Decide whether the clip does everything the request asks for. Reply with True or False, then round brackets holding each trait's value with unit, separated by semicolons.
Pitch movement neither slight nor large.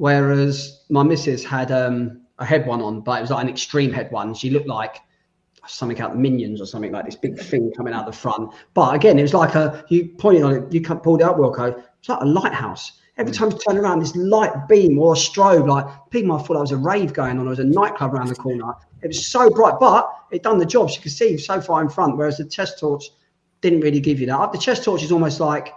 True (5.0 semitones)